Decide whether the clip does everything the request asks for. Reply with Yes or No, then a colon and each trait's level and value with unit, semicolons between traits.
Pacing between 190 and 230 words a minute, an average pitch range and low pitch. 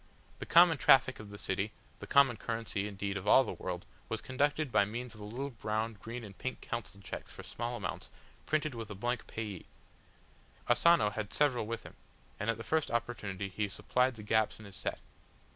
Yes: average, 200 wpm; average, 3.4 semitones; low, 115 Hz